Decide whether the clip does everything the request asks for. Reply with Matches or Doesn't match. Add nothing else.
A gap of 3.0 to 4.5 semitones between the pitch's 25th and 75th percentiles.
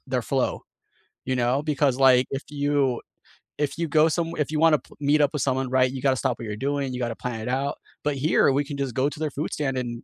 Doesn't match